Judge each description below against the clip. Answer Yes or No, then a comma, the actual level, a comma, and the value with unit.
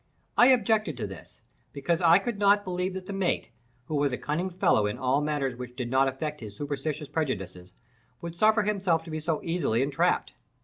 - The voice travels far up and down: Yes, wide, 5.9 semitones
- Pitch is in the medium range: Yes, medium, 155 Hz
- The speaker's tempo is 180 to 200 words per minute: Yes, average, 195 wpm